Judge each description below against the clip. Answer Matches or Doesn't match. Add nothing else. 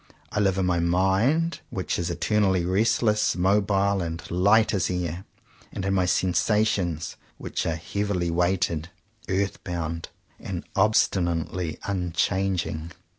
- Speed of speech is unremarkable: Doesn't match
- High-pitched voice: Doesn't match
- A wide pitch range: Doesn't match